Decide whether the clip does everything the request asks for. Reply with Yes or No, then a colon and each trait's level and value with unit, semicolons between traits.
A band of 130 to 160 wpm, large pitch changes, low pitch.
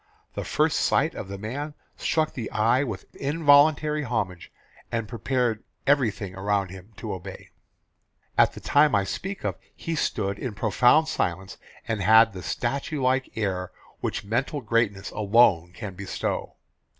Yes: average, 150 wpm; wide, 5.7 semitones; low, 110 Hz